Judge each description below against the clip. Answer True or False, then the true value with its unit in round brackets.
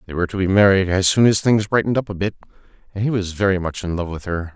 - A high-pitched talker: False (95 Hz)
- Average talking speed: False (290 wpm)